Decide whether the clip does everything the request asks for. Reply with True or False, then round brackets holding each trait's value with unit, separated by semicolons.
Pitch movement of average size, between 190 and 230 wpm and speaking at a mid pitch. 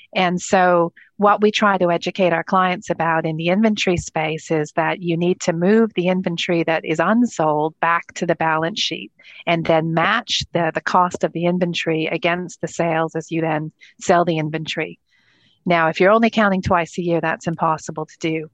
False (2.2 semitones; 195 wpm; 170 Hz)